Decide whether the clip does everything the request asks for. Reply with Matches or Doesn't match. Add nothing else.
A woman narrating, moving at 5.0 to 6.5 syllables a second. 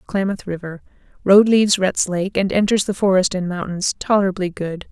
Matches